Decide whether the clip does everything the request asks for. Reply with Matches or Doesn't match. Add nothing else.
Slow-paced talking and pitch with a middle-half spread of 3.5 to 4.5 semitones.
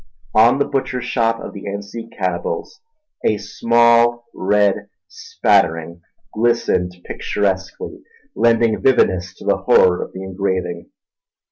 Matches